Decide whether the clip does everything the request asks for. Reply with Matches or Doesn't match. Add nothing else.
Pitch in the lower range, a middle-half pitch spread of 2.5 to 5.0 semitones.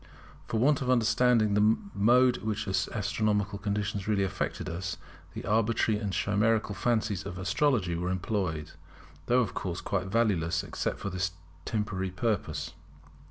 Matches